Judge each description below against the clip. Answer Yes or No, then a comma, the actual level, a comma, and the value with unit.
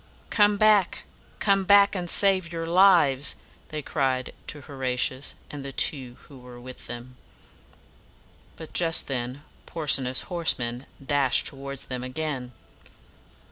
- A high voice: No, medium, 140 Hz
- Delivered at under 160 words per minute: Yes, average, 140 wpm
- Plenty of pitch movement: No, average, 5.0 semitones